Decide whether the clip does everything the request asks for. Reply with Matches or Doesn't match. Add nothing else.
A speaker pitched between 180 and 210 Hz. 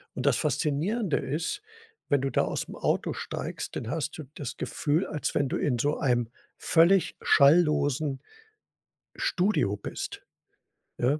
Doesn't match